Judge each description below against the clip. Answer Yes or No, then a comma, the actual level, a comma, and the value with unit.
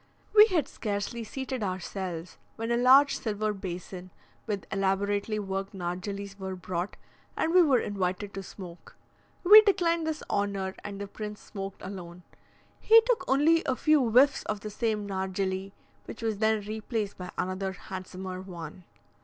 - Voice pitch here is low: No, high, 200 Hz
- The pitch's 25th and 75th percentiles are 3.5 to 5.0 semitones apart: Yes, average, 3.9 semitones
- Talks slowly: No, average, 155 wpm